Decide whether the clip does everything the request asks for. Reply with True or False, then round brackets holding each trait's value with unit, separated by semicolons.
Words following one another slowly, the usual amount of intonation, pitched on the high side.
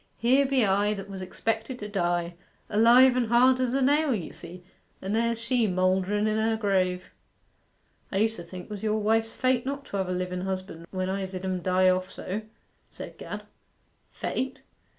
False (190 wpm; 4.0 semitones; 205 Hz)